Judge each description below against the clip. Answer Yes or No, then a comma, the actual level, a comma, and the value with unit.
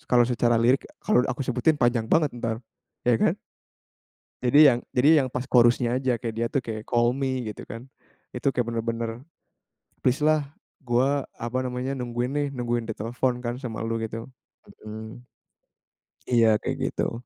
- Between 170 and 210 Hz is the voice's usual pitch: No, low, 120 Hz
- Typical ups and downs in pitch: No, narrow, 1.9 semitones